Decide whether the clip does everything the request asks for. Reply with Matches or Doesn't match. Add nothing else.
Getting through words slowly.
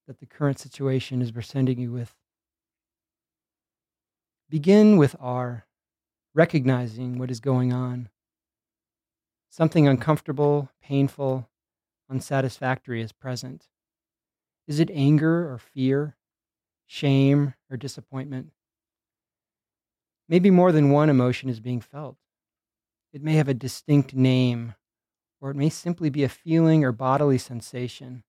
Matches